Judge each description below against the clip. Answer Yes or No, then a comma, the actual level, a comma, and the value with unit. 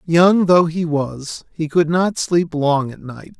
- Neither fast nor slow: Yes, average, 195 wpm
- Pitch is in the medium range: Yes, medium, 160 Hz